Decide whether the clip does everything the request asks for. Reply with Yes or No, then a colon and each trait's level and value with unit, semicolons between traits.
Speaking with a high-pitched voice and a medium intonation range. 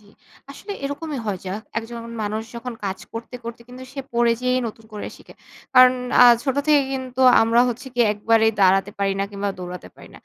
Yes: high, 230 Hz; average, 3.6 semitones